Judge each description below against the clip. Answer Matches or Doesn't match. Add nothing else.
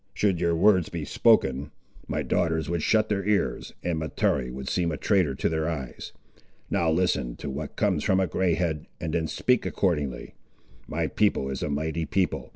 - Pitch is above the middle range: Doesn't match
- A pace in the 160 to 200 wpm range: Matches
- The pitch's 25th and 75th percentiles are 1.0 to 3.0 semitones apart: Doesn't match